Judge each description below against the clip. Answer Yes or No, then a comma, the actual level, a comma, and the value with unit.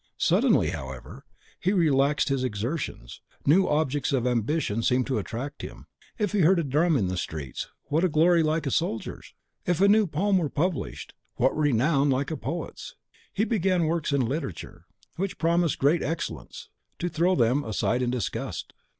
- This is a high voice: No, medium, 150 Hz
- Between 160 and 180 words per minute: Yes, average, 165 wpm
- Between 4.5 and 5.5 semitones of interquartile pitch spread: Yes, average, 5.1 semitones